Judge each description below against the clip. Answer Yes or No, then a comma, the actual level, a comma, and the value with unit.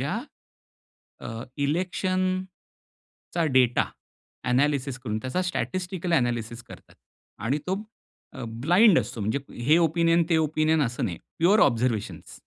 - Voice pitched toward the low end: No, medium, 150 Hz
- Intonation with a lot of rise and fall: Yes, wide, 6.5 semitones